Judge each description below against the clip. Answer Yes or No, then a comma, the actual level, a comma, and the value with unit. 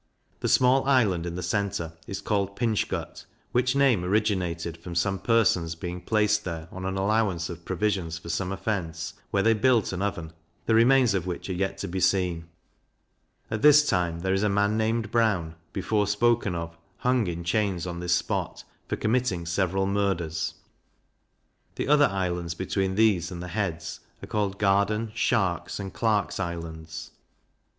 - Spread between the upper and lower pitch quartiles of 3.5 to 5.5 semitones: Yes, average, 3.8 semitones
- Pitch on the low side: Yes, very low, 95 Hz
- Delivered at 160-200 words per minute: Yes, average, 170 wpm